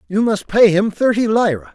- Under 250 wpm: Yes, fast, 205 wpm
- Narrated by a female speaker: No, male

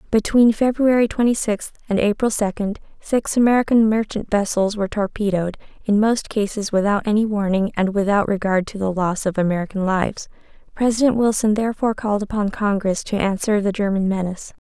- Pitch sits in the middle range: No, high, 210 Hz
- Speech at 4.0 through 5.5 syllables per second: No, 5.7 syllables/s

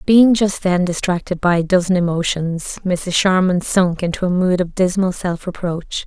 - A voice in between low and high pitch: Yes, medium, 180 Hz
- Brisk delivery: No, average, 180 wpm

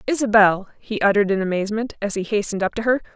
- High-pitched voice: Yes, high, 215 Hz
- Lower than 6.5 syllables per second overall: No, 7.2 syllables/s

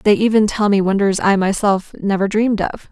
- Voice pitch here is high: Yes, high, 200 Hz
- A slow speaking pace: No, fast, 205 wpm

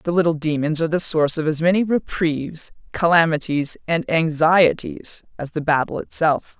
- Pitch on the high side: No, medium, 160 Hz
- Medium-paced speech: Yes, average, 155 wpm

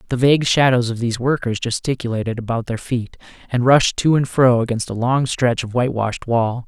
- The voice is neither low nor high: No, low, 120 Hz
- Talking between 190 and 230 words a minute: Yes, fast, 205 wpm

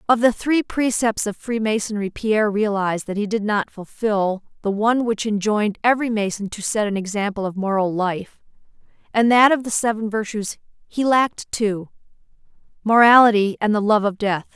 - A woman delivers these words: Yes, female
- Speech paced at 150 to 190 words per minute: Yes, average, 165 wpm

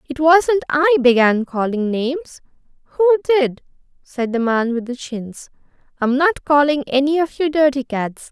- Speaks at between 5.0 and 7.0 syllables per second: No, 4.7 syllables/s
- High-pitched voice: Yes, very high, 280 Hz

